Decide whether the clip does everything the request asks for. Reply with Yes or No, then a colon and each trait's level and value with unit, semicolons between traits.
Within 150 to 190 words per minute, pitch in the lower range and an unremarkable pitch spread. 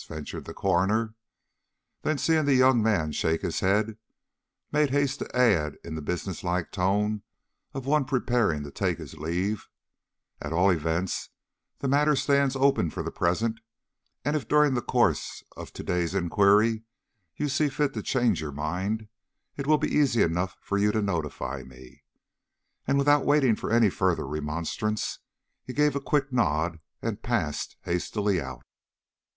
No: average, 160 wpm; low, 105 Hz; wide, 7.5 semitones